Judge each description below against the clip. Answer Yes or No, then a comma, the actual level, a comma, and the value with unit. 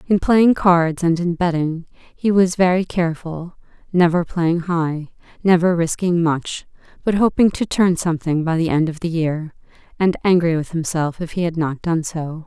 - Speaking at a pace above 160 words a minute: Yes, average, 180 wpm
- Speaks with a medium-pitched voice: Yes, medium, 170 Hz